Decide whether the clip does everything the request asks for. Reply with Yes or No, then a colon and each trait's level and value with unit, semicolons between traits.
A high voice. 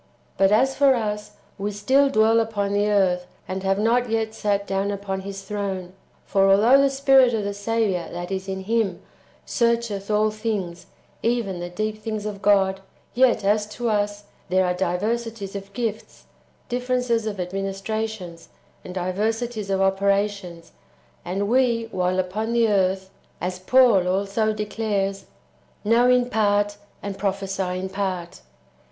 Yes: high, 205 Hz